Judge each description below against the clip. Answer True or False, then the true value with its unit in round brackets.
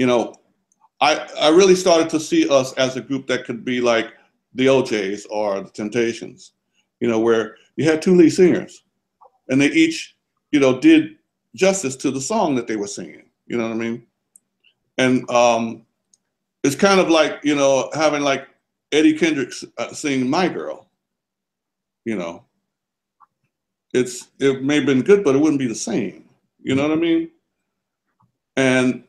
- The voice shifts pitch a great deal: True (5.7 semitones)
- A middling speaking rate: True (170 wpm)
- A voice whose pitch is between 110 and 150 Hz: True (135 Hz)